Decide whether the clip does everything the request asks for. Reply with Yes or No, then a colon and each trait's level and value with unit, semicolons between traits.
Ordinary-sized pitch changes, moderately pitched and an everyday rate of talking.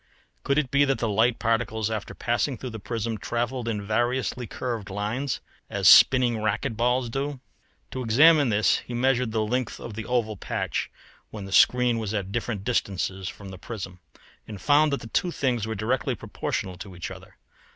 No: average, 3.0 semitones; low, 115 Hz; average, 185 wpm